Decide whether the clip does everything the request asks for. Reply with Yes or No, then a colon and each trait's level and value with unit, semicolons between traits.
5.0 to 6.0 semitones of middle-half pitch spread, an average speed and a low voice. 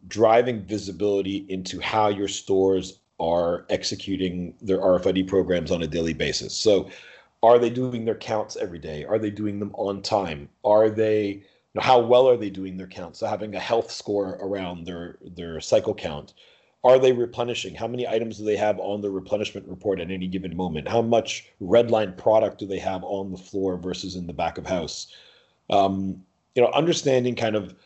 No: average, 3.2 semitones; average, 190 wpm; low, 100 Hz